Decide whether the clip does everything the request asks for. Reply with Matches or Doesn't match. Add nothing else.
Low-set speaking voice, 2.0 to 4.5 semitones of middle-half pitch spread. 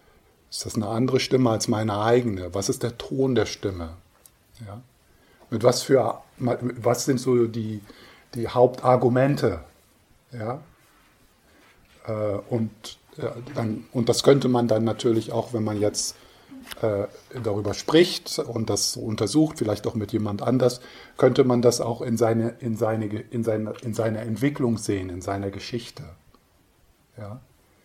Matches